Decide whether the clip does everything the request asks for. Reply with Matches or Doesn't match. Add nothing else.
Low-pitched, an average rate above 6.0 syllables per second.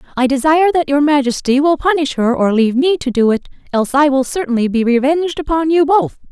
Doesn't match